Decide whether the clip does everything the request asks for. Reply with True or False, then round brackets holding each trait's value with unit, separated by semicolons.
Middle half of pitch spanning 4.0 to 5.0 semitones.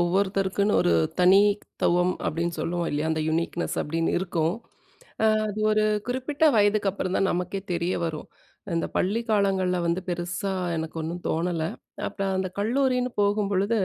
False (3.0 semitones)